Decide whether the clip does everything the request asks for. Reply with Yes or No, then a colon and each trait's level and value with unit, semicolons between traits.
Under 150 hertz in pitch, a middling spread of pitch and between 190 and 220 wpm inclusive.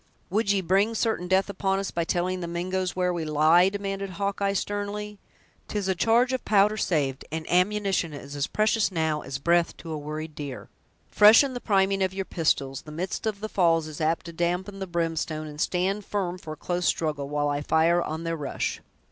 No: medium, 180 Hz; average, 3.8 semitones; average, 200 wpm